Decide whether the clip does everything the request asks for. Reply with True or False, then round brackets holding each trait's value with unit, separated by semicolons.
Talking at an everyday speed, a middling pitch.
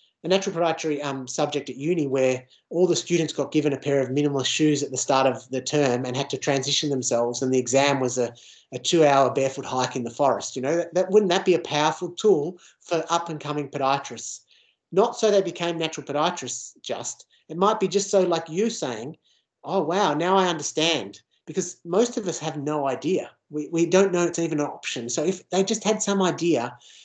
False (215 wpm; 150 Hz)